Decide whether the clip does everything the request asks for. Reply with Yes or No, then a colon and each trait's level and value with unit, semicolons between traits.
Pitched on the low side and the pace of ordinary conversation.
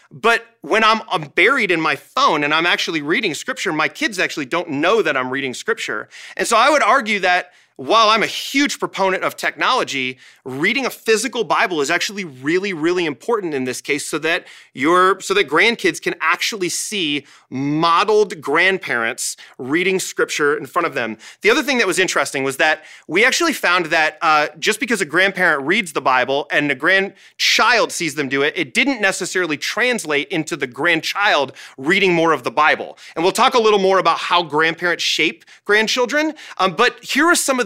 No: high, 190 Hz; average, 190 wpm